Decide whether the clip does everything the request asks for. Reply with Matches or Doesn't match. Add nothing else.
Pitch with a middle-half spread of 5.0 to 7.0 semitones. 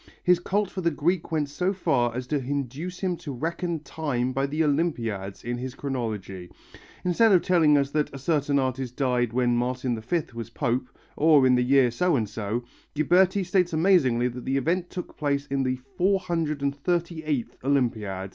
Matches